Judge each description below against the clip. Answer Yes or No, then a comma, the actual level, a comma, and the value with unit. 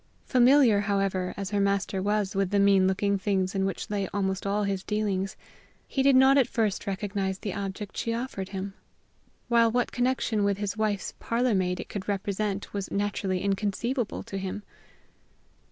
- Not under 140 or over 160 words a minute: No, average, 170 wpm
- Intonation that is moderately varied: No, narrow, 1.9 semitones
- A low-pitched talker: No, high, 200 Hz